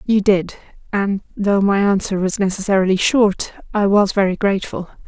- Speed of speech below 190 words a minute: Yes, average, 140 wpm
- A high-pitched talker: Yes, high, 200 Hz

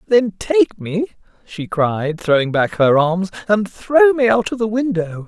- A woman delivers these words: No, male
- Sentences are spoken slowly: No, average, 180 wpm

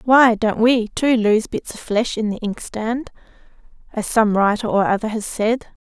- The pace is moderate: Yes, average, 185 wpm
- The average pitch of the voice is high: Yes, high, 225 Hz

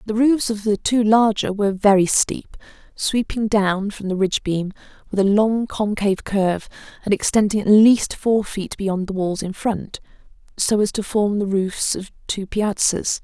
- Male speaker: No, female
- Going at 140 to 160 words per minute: No, average, 175 wpm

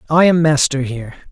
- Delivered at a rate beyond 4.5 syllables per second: Yes, 6.3 syllables/s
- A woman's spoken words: No, male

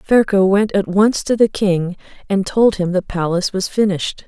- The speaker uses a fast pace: No, average, 195 wpm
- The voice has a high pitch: Yes, high, 195 Hz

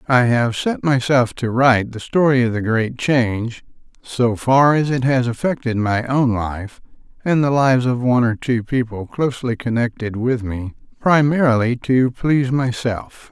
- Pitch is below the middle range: Yes, low, 125 Hz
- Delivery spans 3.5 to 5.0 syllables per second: Yes, 4.6 syllables/s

